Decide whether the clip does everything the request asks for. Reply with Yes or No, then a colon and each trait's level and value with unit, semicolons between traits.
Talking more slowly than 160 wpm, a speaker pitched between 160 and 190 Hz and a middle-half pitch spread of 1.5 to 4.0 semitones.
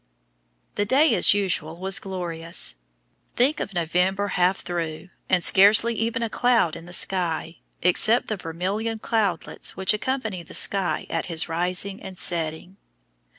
Yes: average, 145 wpm; medium, 185 Hz; average, 3.6 semitones